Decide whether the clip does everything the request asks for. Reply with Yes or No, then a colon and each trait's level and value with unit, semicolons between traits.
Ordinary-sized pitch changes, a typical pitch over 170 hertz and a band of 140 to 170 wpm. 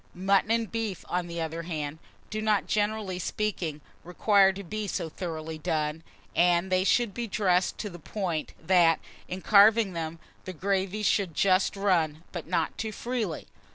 Yes: average, 3.8 semitones; medium, 185 Hz; average, 165 wpm